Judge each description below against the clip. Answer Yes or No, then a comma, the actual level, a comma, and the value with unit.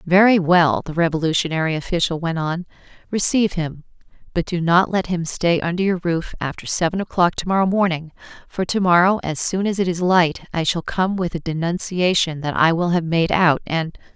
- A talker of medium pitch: Yes, medium, 175 Hz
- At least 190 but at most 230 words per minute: Yes, average, 195 wpm